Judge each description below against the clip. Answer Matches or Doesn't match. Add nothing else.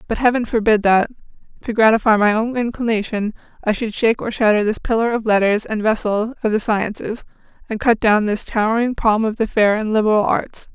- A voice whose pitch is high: Matches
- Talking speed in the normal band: Matches